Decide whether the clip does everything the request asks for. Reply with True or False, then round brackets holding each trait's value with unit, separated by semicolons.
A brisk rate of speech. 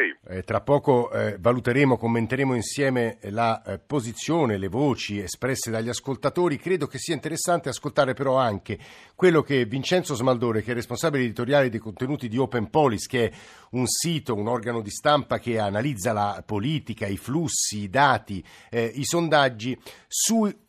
False (160 wpm)